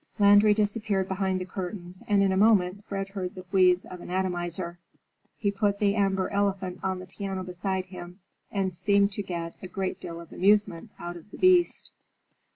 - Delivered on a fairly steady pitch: Yes, narrow, 1.9 semitones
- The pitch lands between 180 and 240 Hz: Yes, high, 190 Hz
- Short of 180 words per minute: No, average, 185 wpm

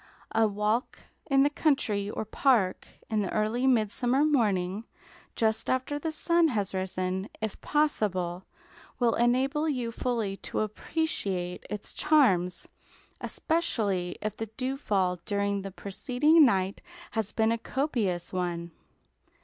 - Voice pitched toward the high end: Yes, high, 220 Hz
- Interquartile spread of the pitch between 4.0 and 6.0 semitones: Yes, wide, 5.4 semitones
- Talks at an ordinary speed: No, slow, 125 wpm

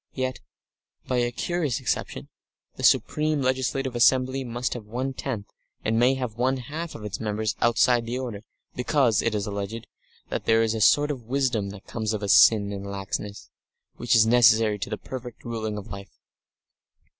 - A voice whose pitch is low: Yes, low, 115 Hz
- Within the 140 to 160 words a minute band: No, average, 170 wpm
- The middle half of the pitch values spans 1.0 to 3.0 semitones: No, average, 3.4 semitones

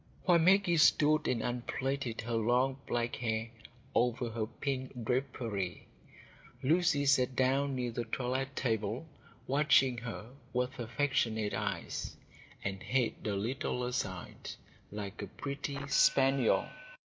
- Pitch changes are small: No, average, 3.2 semitones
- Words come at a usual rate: No, slow, 120 wpm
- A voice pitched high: No, low, 125 Hz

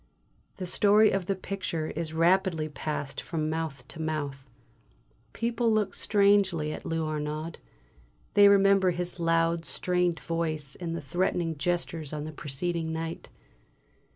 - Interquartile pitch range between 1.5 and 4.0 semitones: Yes, average, 3.1 semitones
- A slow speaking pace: Yes, slow, 130 wpm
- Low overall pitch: No, medium, 165 Hz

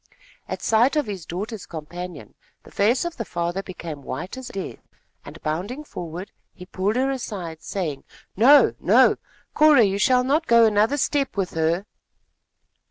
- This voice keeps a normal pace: Yes, average, 160 wpm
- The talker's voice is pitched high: Yes, high, 200 Hz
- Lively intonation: Yes, wide, 6.3 semitones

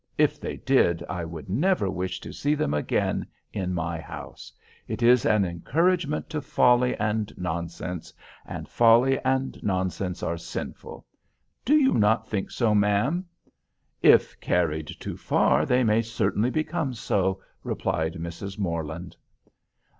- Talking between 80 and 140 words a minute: Yes, slow, 135 wpm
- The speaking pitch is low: Yes, low, 100 Hz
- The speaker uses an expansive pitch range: Yes, wide, 6.6 semitones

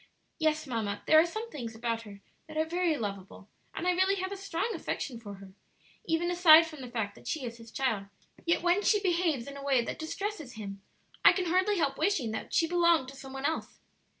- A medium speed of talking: No, fast, 225 wpm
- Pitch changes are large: Yes, wide, 7.1 semitones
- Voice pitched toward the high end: Yes, very high, 310 Hz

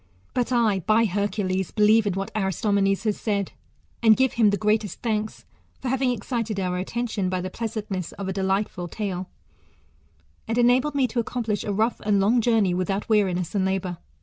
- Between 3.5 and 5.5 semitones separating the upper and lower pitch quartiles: No, average, 3.0 semitones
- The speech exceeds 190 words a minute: No, average, 180 wpm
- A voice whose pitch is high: Yes, high, 210 Hz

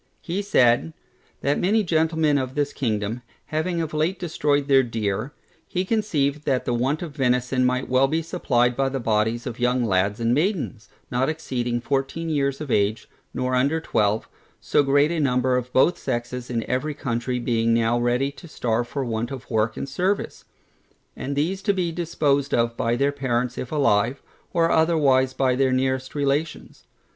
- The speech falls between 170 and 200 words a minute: Yes, average, 175 wpm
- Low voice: Yes, low, 130 Hz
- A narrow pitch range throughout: No, average, 4.0 semitones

